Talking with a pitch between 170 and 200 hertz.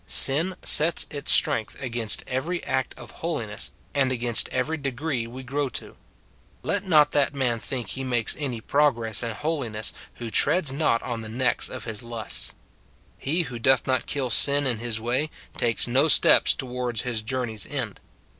No: low, 130 Hz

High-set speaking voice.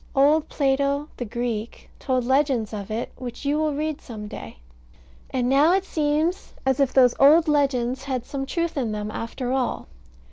Yes: very high, 270 Hz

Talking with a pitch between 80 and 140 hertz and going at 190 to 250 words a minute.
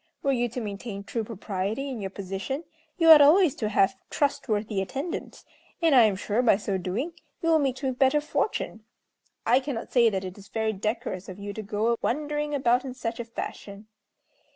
No: high, 235 Hz; average, 195 wpm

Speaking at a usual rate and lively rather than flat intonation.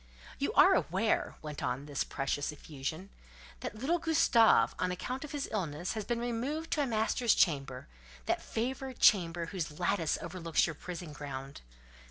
Yes: average, 155 wpm; wide, 8.2 semitones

